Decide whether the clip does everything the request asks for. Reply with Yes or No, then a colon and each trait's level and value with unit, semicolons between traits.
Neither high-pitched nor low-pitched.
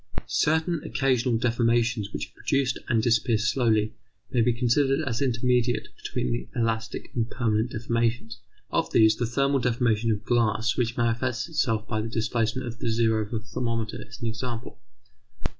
No: low, 115 Hz